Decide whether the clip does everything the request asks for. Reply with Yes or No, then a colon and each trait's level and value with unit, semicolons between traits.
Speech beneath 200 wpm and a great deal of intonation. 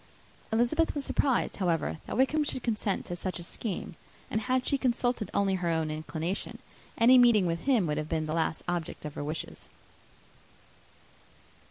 Yes: average, 170 wpm; wide, 7.0 semitones